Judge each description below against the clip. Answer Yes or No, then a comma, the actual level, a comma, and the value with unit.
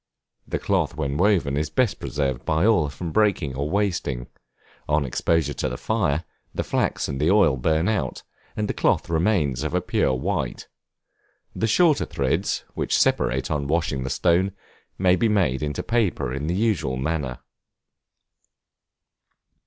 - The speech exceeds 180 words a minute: No, average, 155 wpm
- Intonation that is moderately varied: No, wide, 5.9 semitones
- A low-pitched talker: Yes, very low, 80 Hz